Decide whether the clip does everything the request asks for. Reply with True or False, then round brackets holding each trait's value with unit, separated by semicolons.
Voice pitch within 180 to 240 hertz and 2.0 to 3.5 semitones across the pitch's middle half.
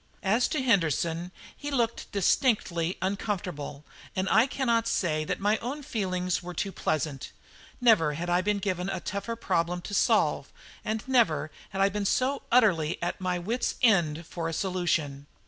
False (190 Hz; 5.0 semitones)